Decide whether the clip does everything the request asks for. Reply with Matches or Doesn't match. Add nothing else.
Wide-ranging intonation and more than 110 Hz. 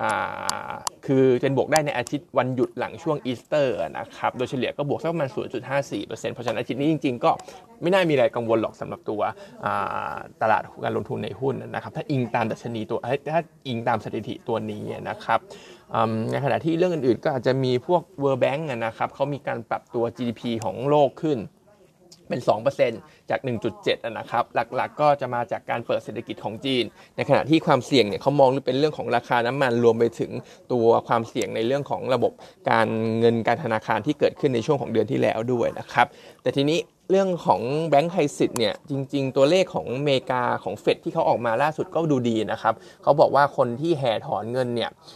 Doesn't match